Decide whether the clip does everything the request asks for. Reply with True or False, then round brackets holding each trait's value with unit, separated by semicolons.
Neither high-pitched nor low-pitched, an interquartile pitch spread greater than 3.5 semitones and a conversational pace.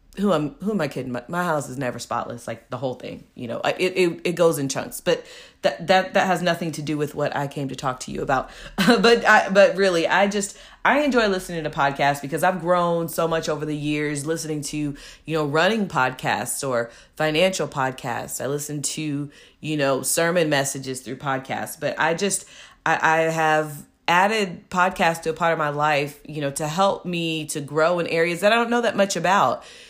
False (160 Hz; 4.2 semitones; 220 wpm)